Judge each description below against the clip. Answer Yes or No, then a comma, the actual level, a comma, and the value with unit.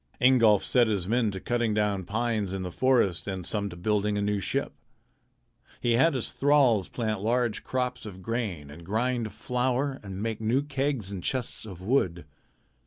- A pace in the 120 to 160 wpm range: No, average, 175 wpm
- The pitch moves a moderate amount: Yes, average, 4.2 semitones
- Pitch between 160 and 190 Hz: No, low, 110 Hz